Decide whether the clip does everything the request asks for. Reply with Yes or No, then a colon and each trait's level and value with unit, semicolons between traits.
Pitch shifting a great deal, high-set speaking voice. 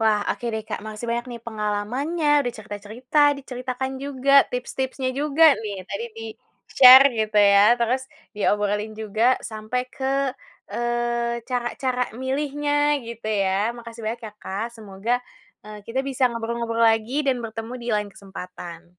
No: average, 3.6 semitones; high, 235 Hz